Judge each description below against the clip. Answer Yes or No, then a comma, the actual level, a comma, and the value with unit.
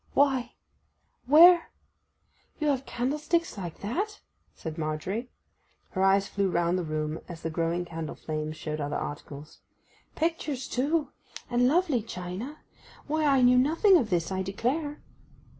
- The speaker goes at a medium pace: No, slow, 125 wpm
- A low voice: No, high, 230 Hz